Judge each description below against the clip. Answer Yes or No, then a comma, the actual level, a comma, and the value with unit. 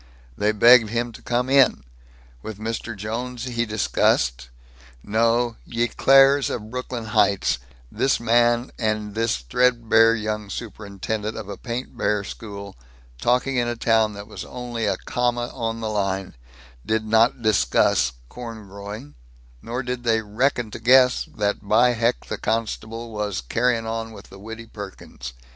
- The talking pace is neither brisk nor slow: Yes, average, 150 wpm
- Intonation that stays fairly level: Yes, narrow, 2.3 semitones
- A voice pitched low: Yes, low, 115 Hz